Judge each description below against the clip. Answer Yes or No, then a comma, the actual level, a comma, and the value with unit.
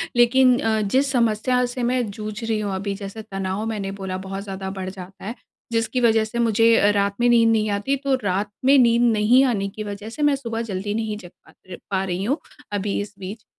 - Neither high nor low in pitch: No, high, 215 Hz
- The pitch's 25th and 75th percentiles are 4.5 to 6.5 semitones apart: No, average, 3.1 semitones